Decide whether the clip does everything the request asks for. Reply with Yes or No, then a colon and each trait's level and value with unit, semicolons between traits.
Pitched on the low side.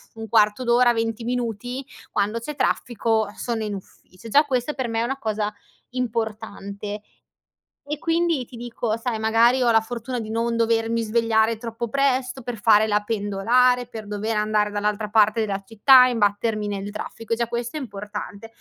No: high, 225 Hz